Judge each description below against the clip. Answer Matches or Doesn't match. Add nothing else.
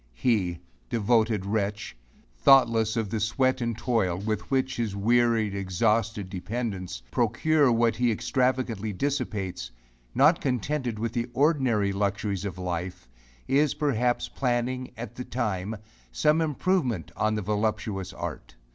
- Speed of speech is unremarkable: Doesn't match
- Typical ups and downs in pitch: Matches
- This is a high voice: Doesn't match